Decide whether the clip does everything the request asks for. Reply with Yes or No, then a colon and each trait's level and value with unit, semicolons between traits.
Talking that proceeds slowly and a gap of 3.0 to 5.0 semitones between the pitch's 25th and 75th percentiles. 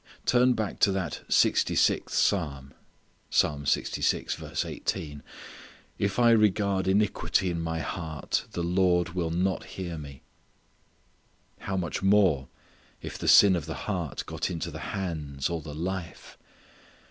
Yes: slow, 125 wpm; average, 3.6 semitones